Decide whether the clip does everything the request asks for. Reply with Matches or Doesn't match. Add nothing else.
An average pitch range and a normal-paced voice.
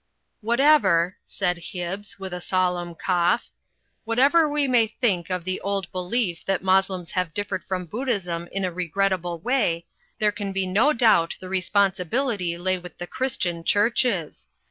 Matches